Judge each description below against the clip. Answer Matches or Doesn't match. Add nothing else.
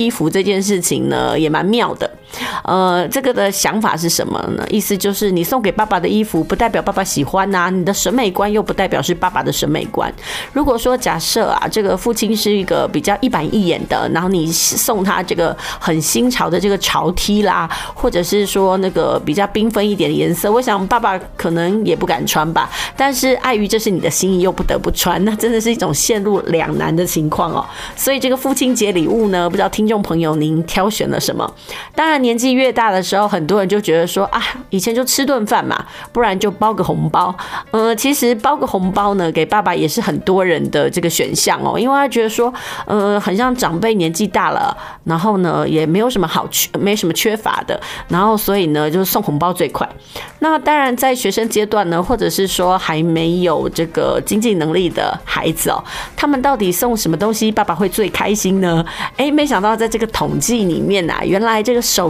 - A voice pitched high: Matches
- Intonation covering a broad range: Doesn't match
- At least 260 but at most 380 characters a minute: Matches